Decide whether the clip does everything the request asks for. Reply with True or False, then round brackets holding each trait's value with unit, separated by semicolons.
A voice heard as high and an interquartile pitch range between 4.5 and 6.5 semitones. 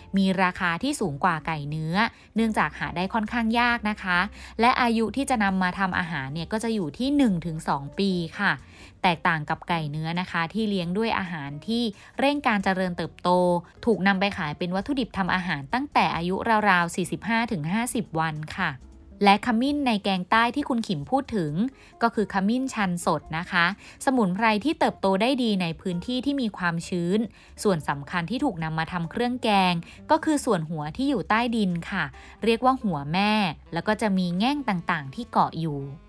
True (195 Hz; 4.8 semitones)